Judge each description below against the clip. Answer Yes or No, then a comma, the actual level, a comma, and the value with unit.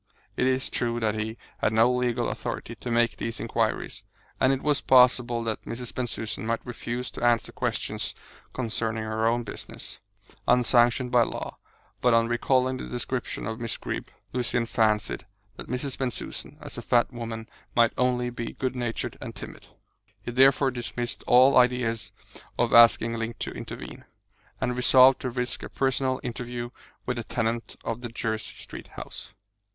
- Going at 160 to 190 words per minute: Yes, average, 165 wpm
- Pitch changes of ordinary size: No, narrow, 1.5 semitones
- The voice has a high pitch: No, low, 120 Hz